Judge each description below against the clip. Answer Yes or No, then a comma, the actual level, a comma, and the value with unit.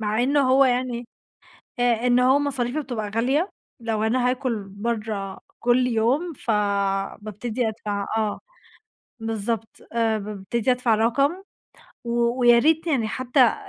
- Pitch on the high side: Yes, high, 235 Hz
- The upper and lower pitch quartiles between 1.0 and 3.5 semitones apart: Yes, average, 2.8 semitones